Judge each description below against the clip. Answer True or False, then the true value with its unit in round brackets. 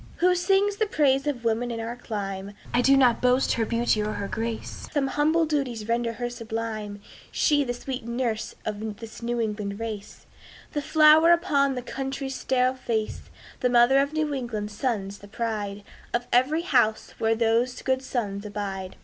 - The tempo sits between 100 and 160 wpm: False (175 wpm)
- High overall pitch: True (240 Hz)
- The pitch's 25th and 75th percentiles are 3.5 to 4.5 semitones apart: True (3.8 semitones)